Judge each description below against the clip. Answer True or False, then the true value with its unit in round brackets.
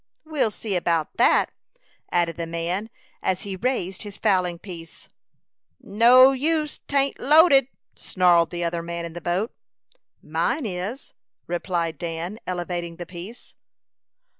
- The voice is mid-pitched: True (180 Hz)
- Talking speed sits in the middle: False (130 wpm)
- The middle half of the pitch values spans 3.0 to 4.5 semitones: False (5.3 semitones)